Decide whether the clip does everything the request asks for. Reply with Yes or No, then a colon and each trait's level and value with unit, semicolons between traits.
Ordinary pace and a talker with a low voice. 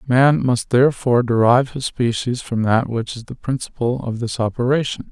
Yes: average, 175 wpm; low, 125 Hz